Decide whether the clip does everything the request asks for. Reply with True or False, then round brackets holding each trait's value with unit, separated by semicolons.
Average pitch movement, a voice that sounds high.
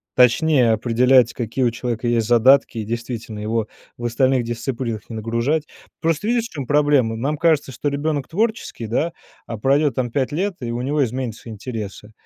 False (3.9 semitones; 125 Hz)